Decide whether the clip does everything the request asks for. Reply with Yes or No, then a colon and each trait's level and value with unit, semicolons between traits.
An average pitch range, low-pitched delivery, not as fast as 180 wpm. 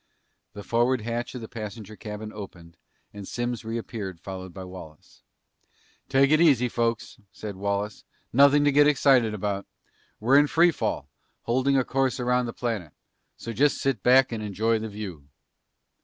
Yes: average, 4.2 semitones; low, 115 Hz; average, 160 wpm